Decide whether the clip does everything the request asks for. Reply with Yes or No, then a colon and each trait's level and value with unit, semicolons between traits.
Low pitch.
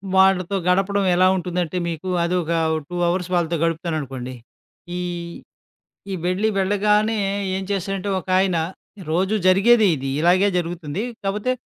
No: medium, 185 Hz